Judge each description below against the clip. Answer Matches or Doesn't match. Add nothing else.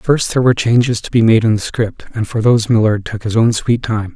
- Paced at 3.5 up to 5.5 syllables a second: Doesn't match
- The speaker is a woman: Doesn't match